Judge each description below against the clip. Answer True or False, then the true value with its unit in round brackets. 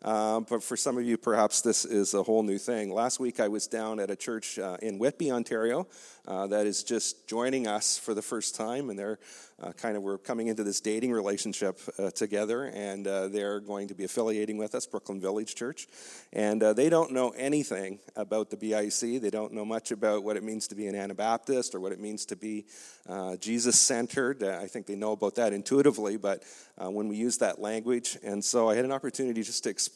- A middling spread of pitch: False (2.3 semitones)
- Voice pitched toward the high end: False (110 Hz)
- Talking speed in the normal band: False (225 wpm)